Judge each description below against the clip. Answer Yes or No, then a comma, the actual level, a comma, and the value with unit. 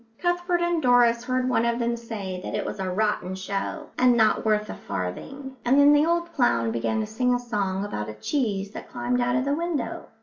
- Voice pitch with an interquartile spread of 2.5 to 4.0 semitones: No, average, 5.2 semitones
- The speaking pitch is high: Yes, high, 235 Hz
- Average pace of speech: No, fast, 225 wpm